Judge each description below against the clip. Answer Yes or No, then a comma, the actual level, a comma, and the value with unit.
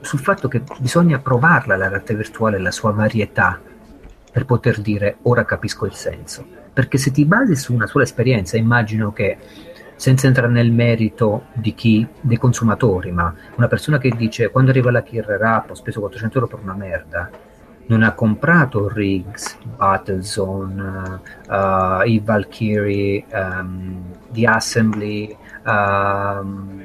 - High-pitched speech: No, low, 110 Hz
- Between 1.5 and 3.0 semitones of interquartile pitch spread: No, average, 3.5 semitones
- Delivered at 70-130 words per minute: No, average, 145 wpm